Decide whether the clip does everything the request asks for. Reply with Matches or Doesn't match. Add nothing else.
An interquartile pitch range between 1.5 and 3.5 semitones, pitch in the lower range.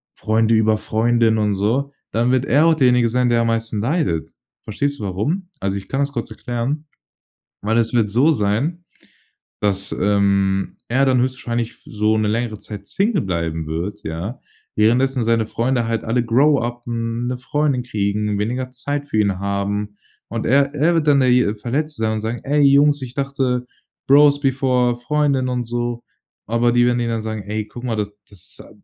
Doesn't match